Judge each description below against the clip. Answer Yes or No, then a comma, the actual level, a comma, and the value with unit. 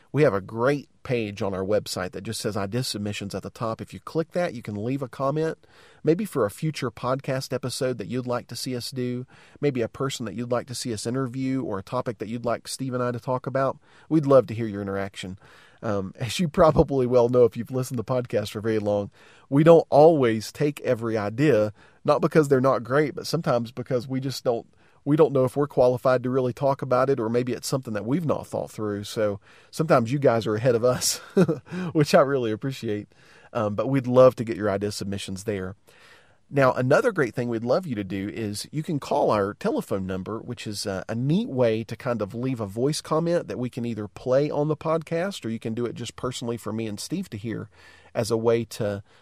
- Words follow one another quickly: Yes, fast, 235 wpm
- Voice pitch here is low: Yes, low, 125 Hz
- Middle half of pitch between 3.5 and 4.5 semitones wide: Yes, average, 3.8 semitones